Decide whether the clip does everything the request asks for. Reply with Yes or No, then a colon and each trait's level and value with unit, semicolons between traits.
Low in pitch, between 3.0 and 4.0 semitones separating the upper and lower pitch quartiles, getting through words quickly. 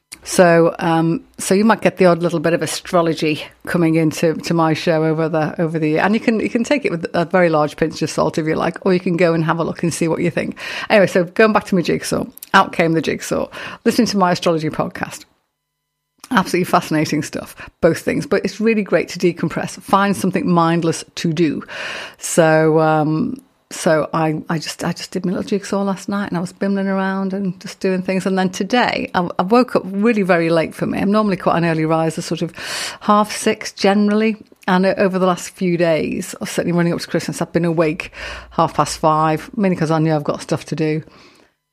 No: medium, 175 Hz; average, 3.6 semitones; fast, 225 wpm